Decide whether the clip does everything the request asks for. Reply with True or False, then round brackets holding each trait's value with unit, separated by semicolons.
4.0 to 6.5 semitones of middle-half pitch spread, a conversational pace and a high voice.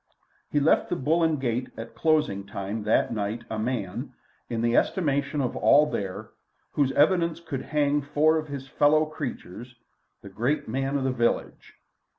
False (4.6 semitones; 165 wpm; 135 Hz)